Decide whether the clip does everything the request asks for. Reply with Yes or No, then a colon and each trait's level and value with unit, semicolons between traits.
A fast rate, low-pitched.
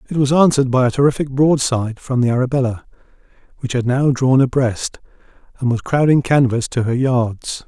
No: average, 170 wpm; low, 130 Hz